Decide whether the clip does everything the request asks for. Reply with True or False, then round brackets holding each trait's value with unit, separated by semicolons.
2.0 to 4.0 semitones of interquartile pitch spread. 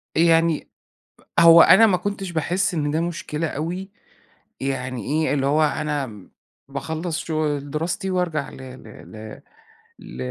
True (3.5 semitones)